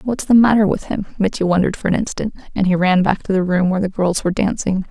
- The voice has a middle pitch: No, high, 195 Hz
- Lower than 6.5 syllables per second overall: No, 6.7 syllables/s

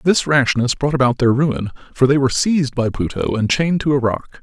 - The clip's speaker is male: Yes, male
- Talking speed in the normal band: No, fast, 230 wpm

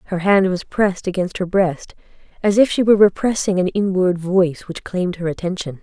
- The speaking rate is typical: Yes, average, 195 wpm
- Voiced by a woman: Yes, female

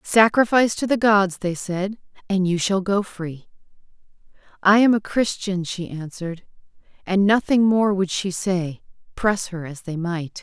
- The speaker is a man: No, female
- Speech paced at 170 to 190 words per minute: No, average, 160 wpm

